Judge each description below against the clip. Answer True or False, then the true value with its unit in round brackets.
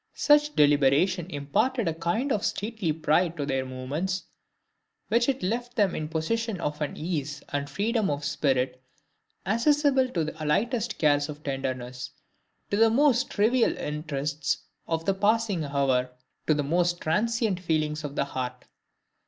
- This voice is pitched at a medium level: True (165 Hz)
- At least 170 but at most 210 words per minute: False (150 wpm)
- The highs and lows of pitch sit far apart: True (7.4 semitones)